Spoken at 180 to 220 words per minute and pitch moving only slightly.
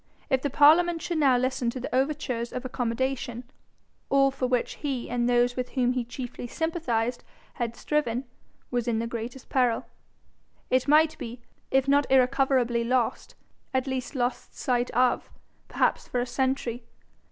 No: average, 155 wpm; narrow, 2.0 semitones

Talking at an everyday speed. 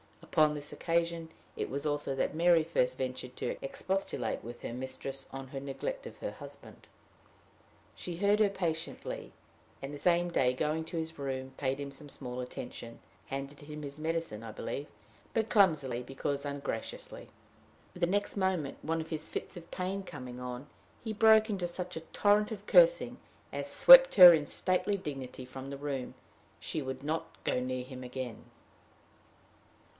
Yes: average, 165 wpm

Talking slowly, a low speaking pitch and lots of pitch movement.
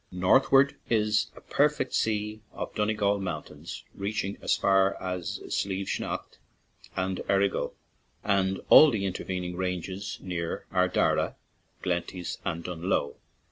No: slow, 120 wpm; very low, 95 Hz; narrow, 2.5 semitones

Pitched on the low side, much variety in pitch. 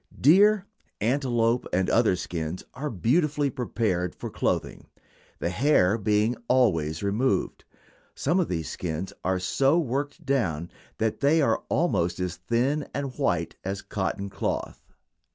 Yes: low, 115 Hz; wide, 7.4 semitones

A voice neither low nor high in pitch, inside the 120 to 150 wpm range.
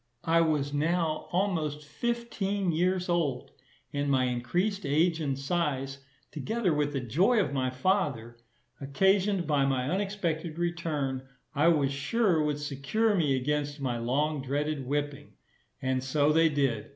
Yes: medium, 150 Hz; average, 140 wpm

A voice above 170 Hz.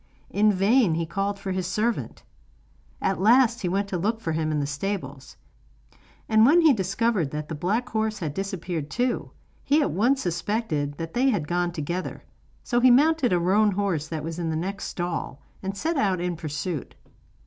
Yes: high, 190 Hz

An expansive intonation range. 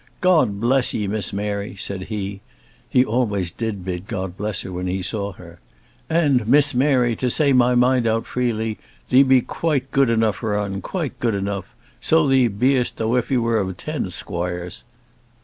No: average, 4.4 semitones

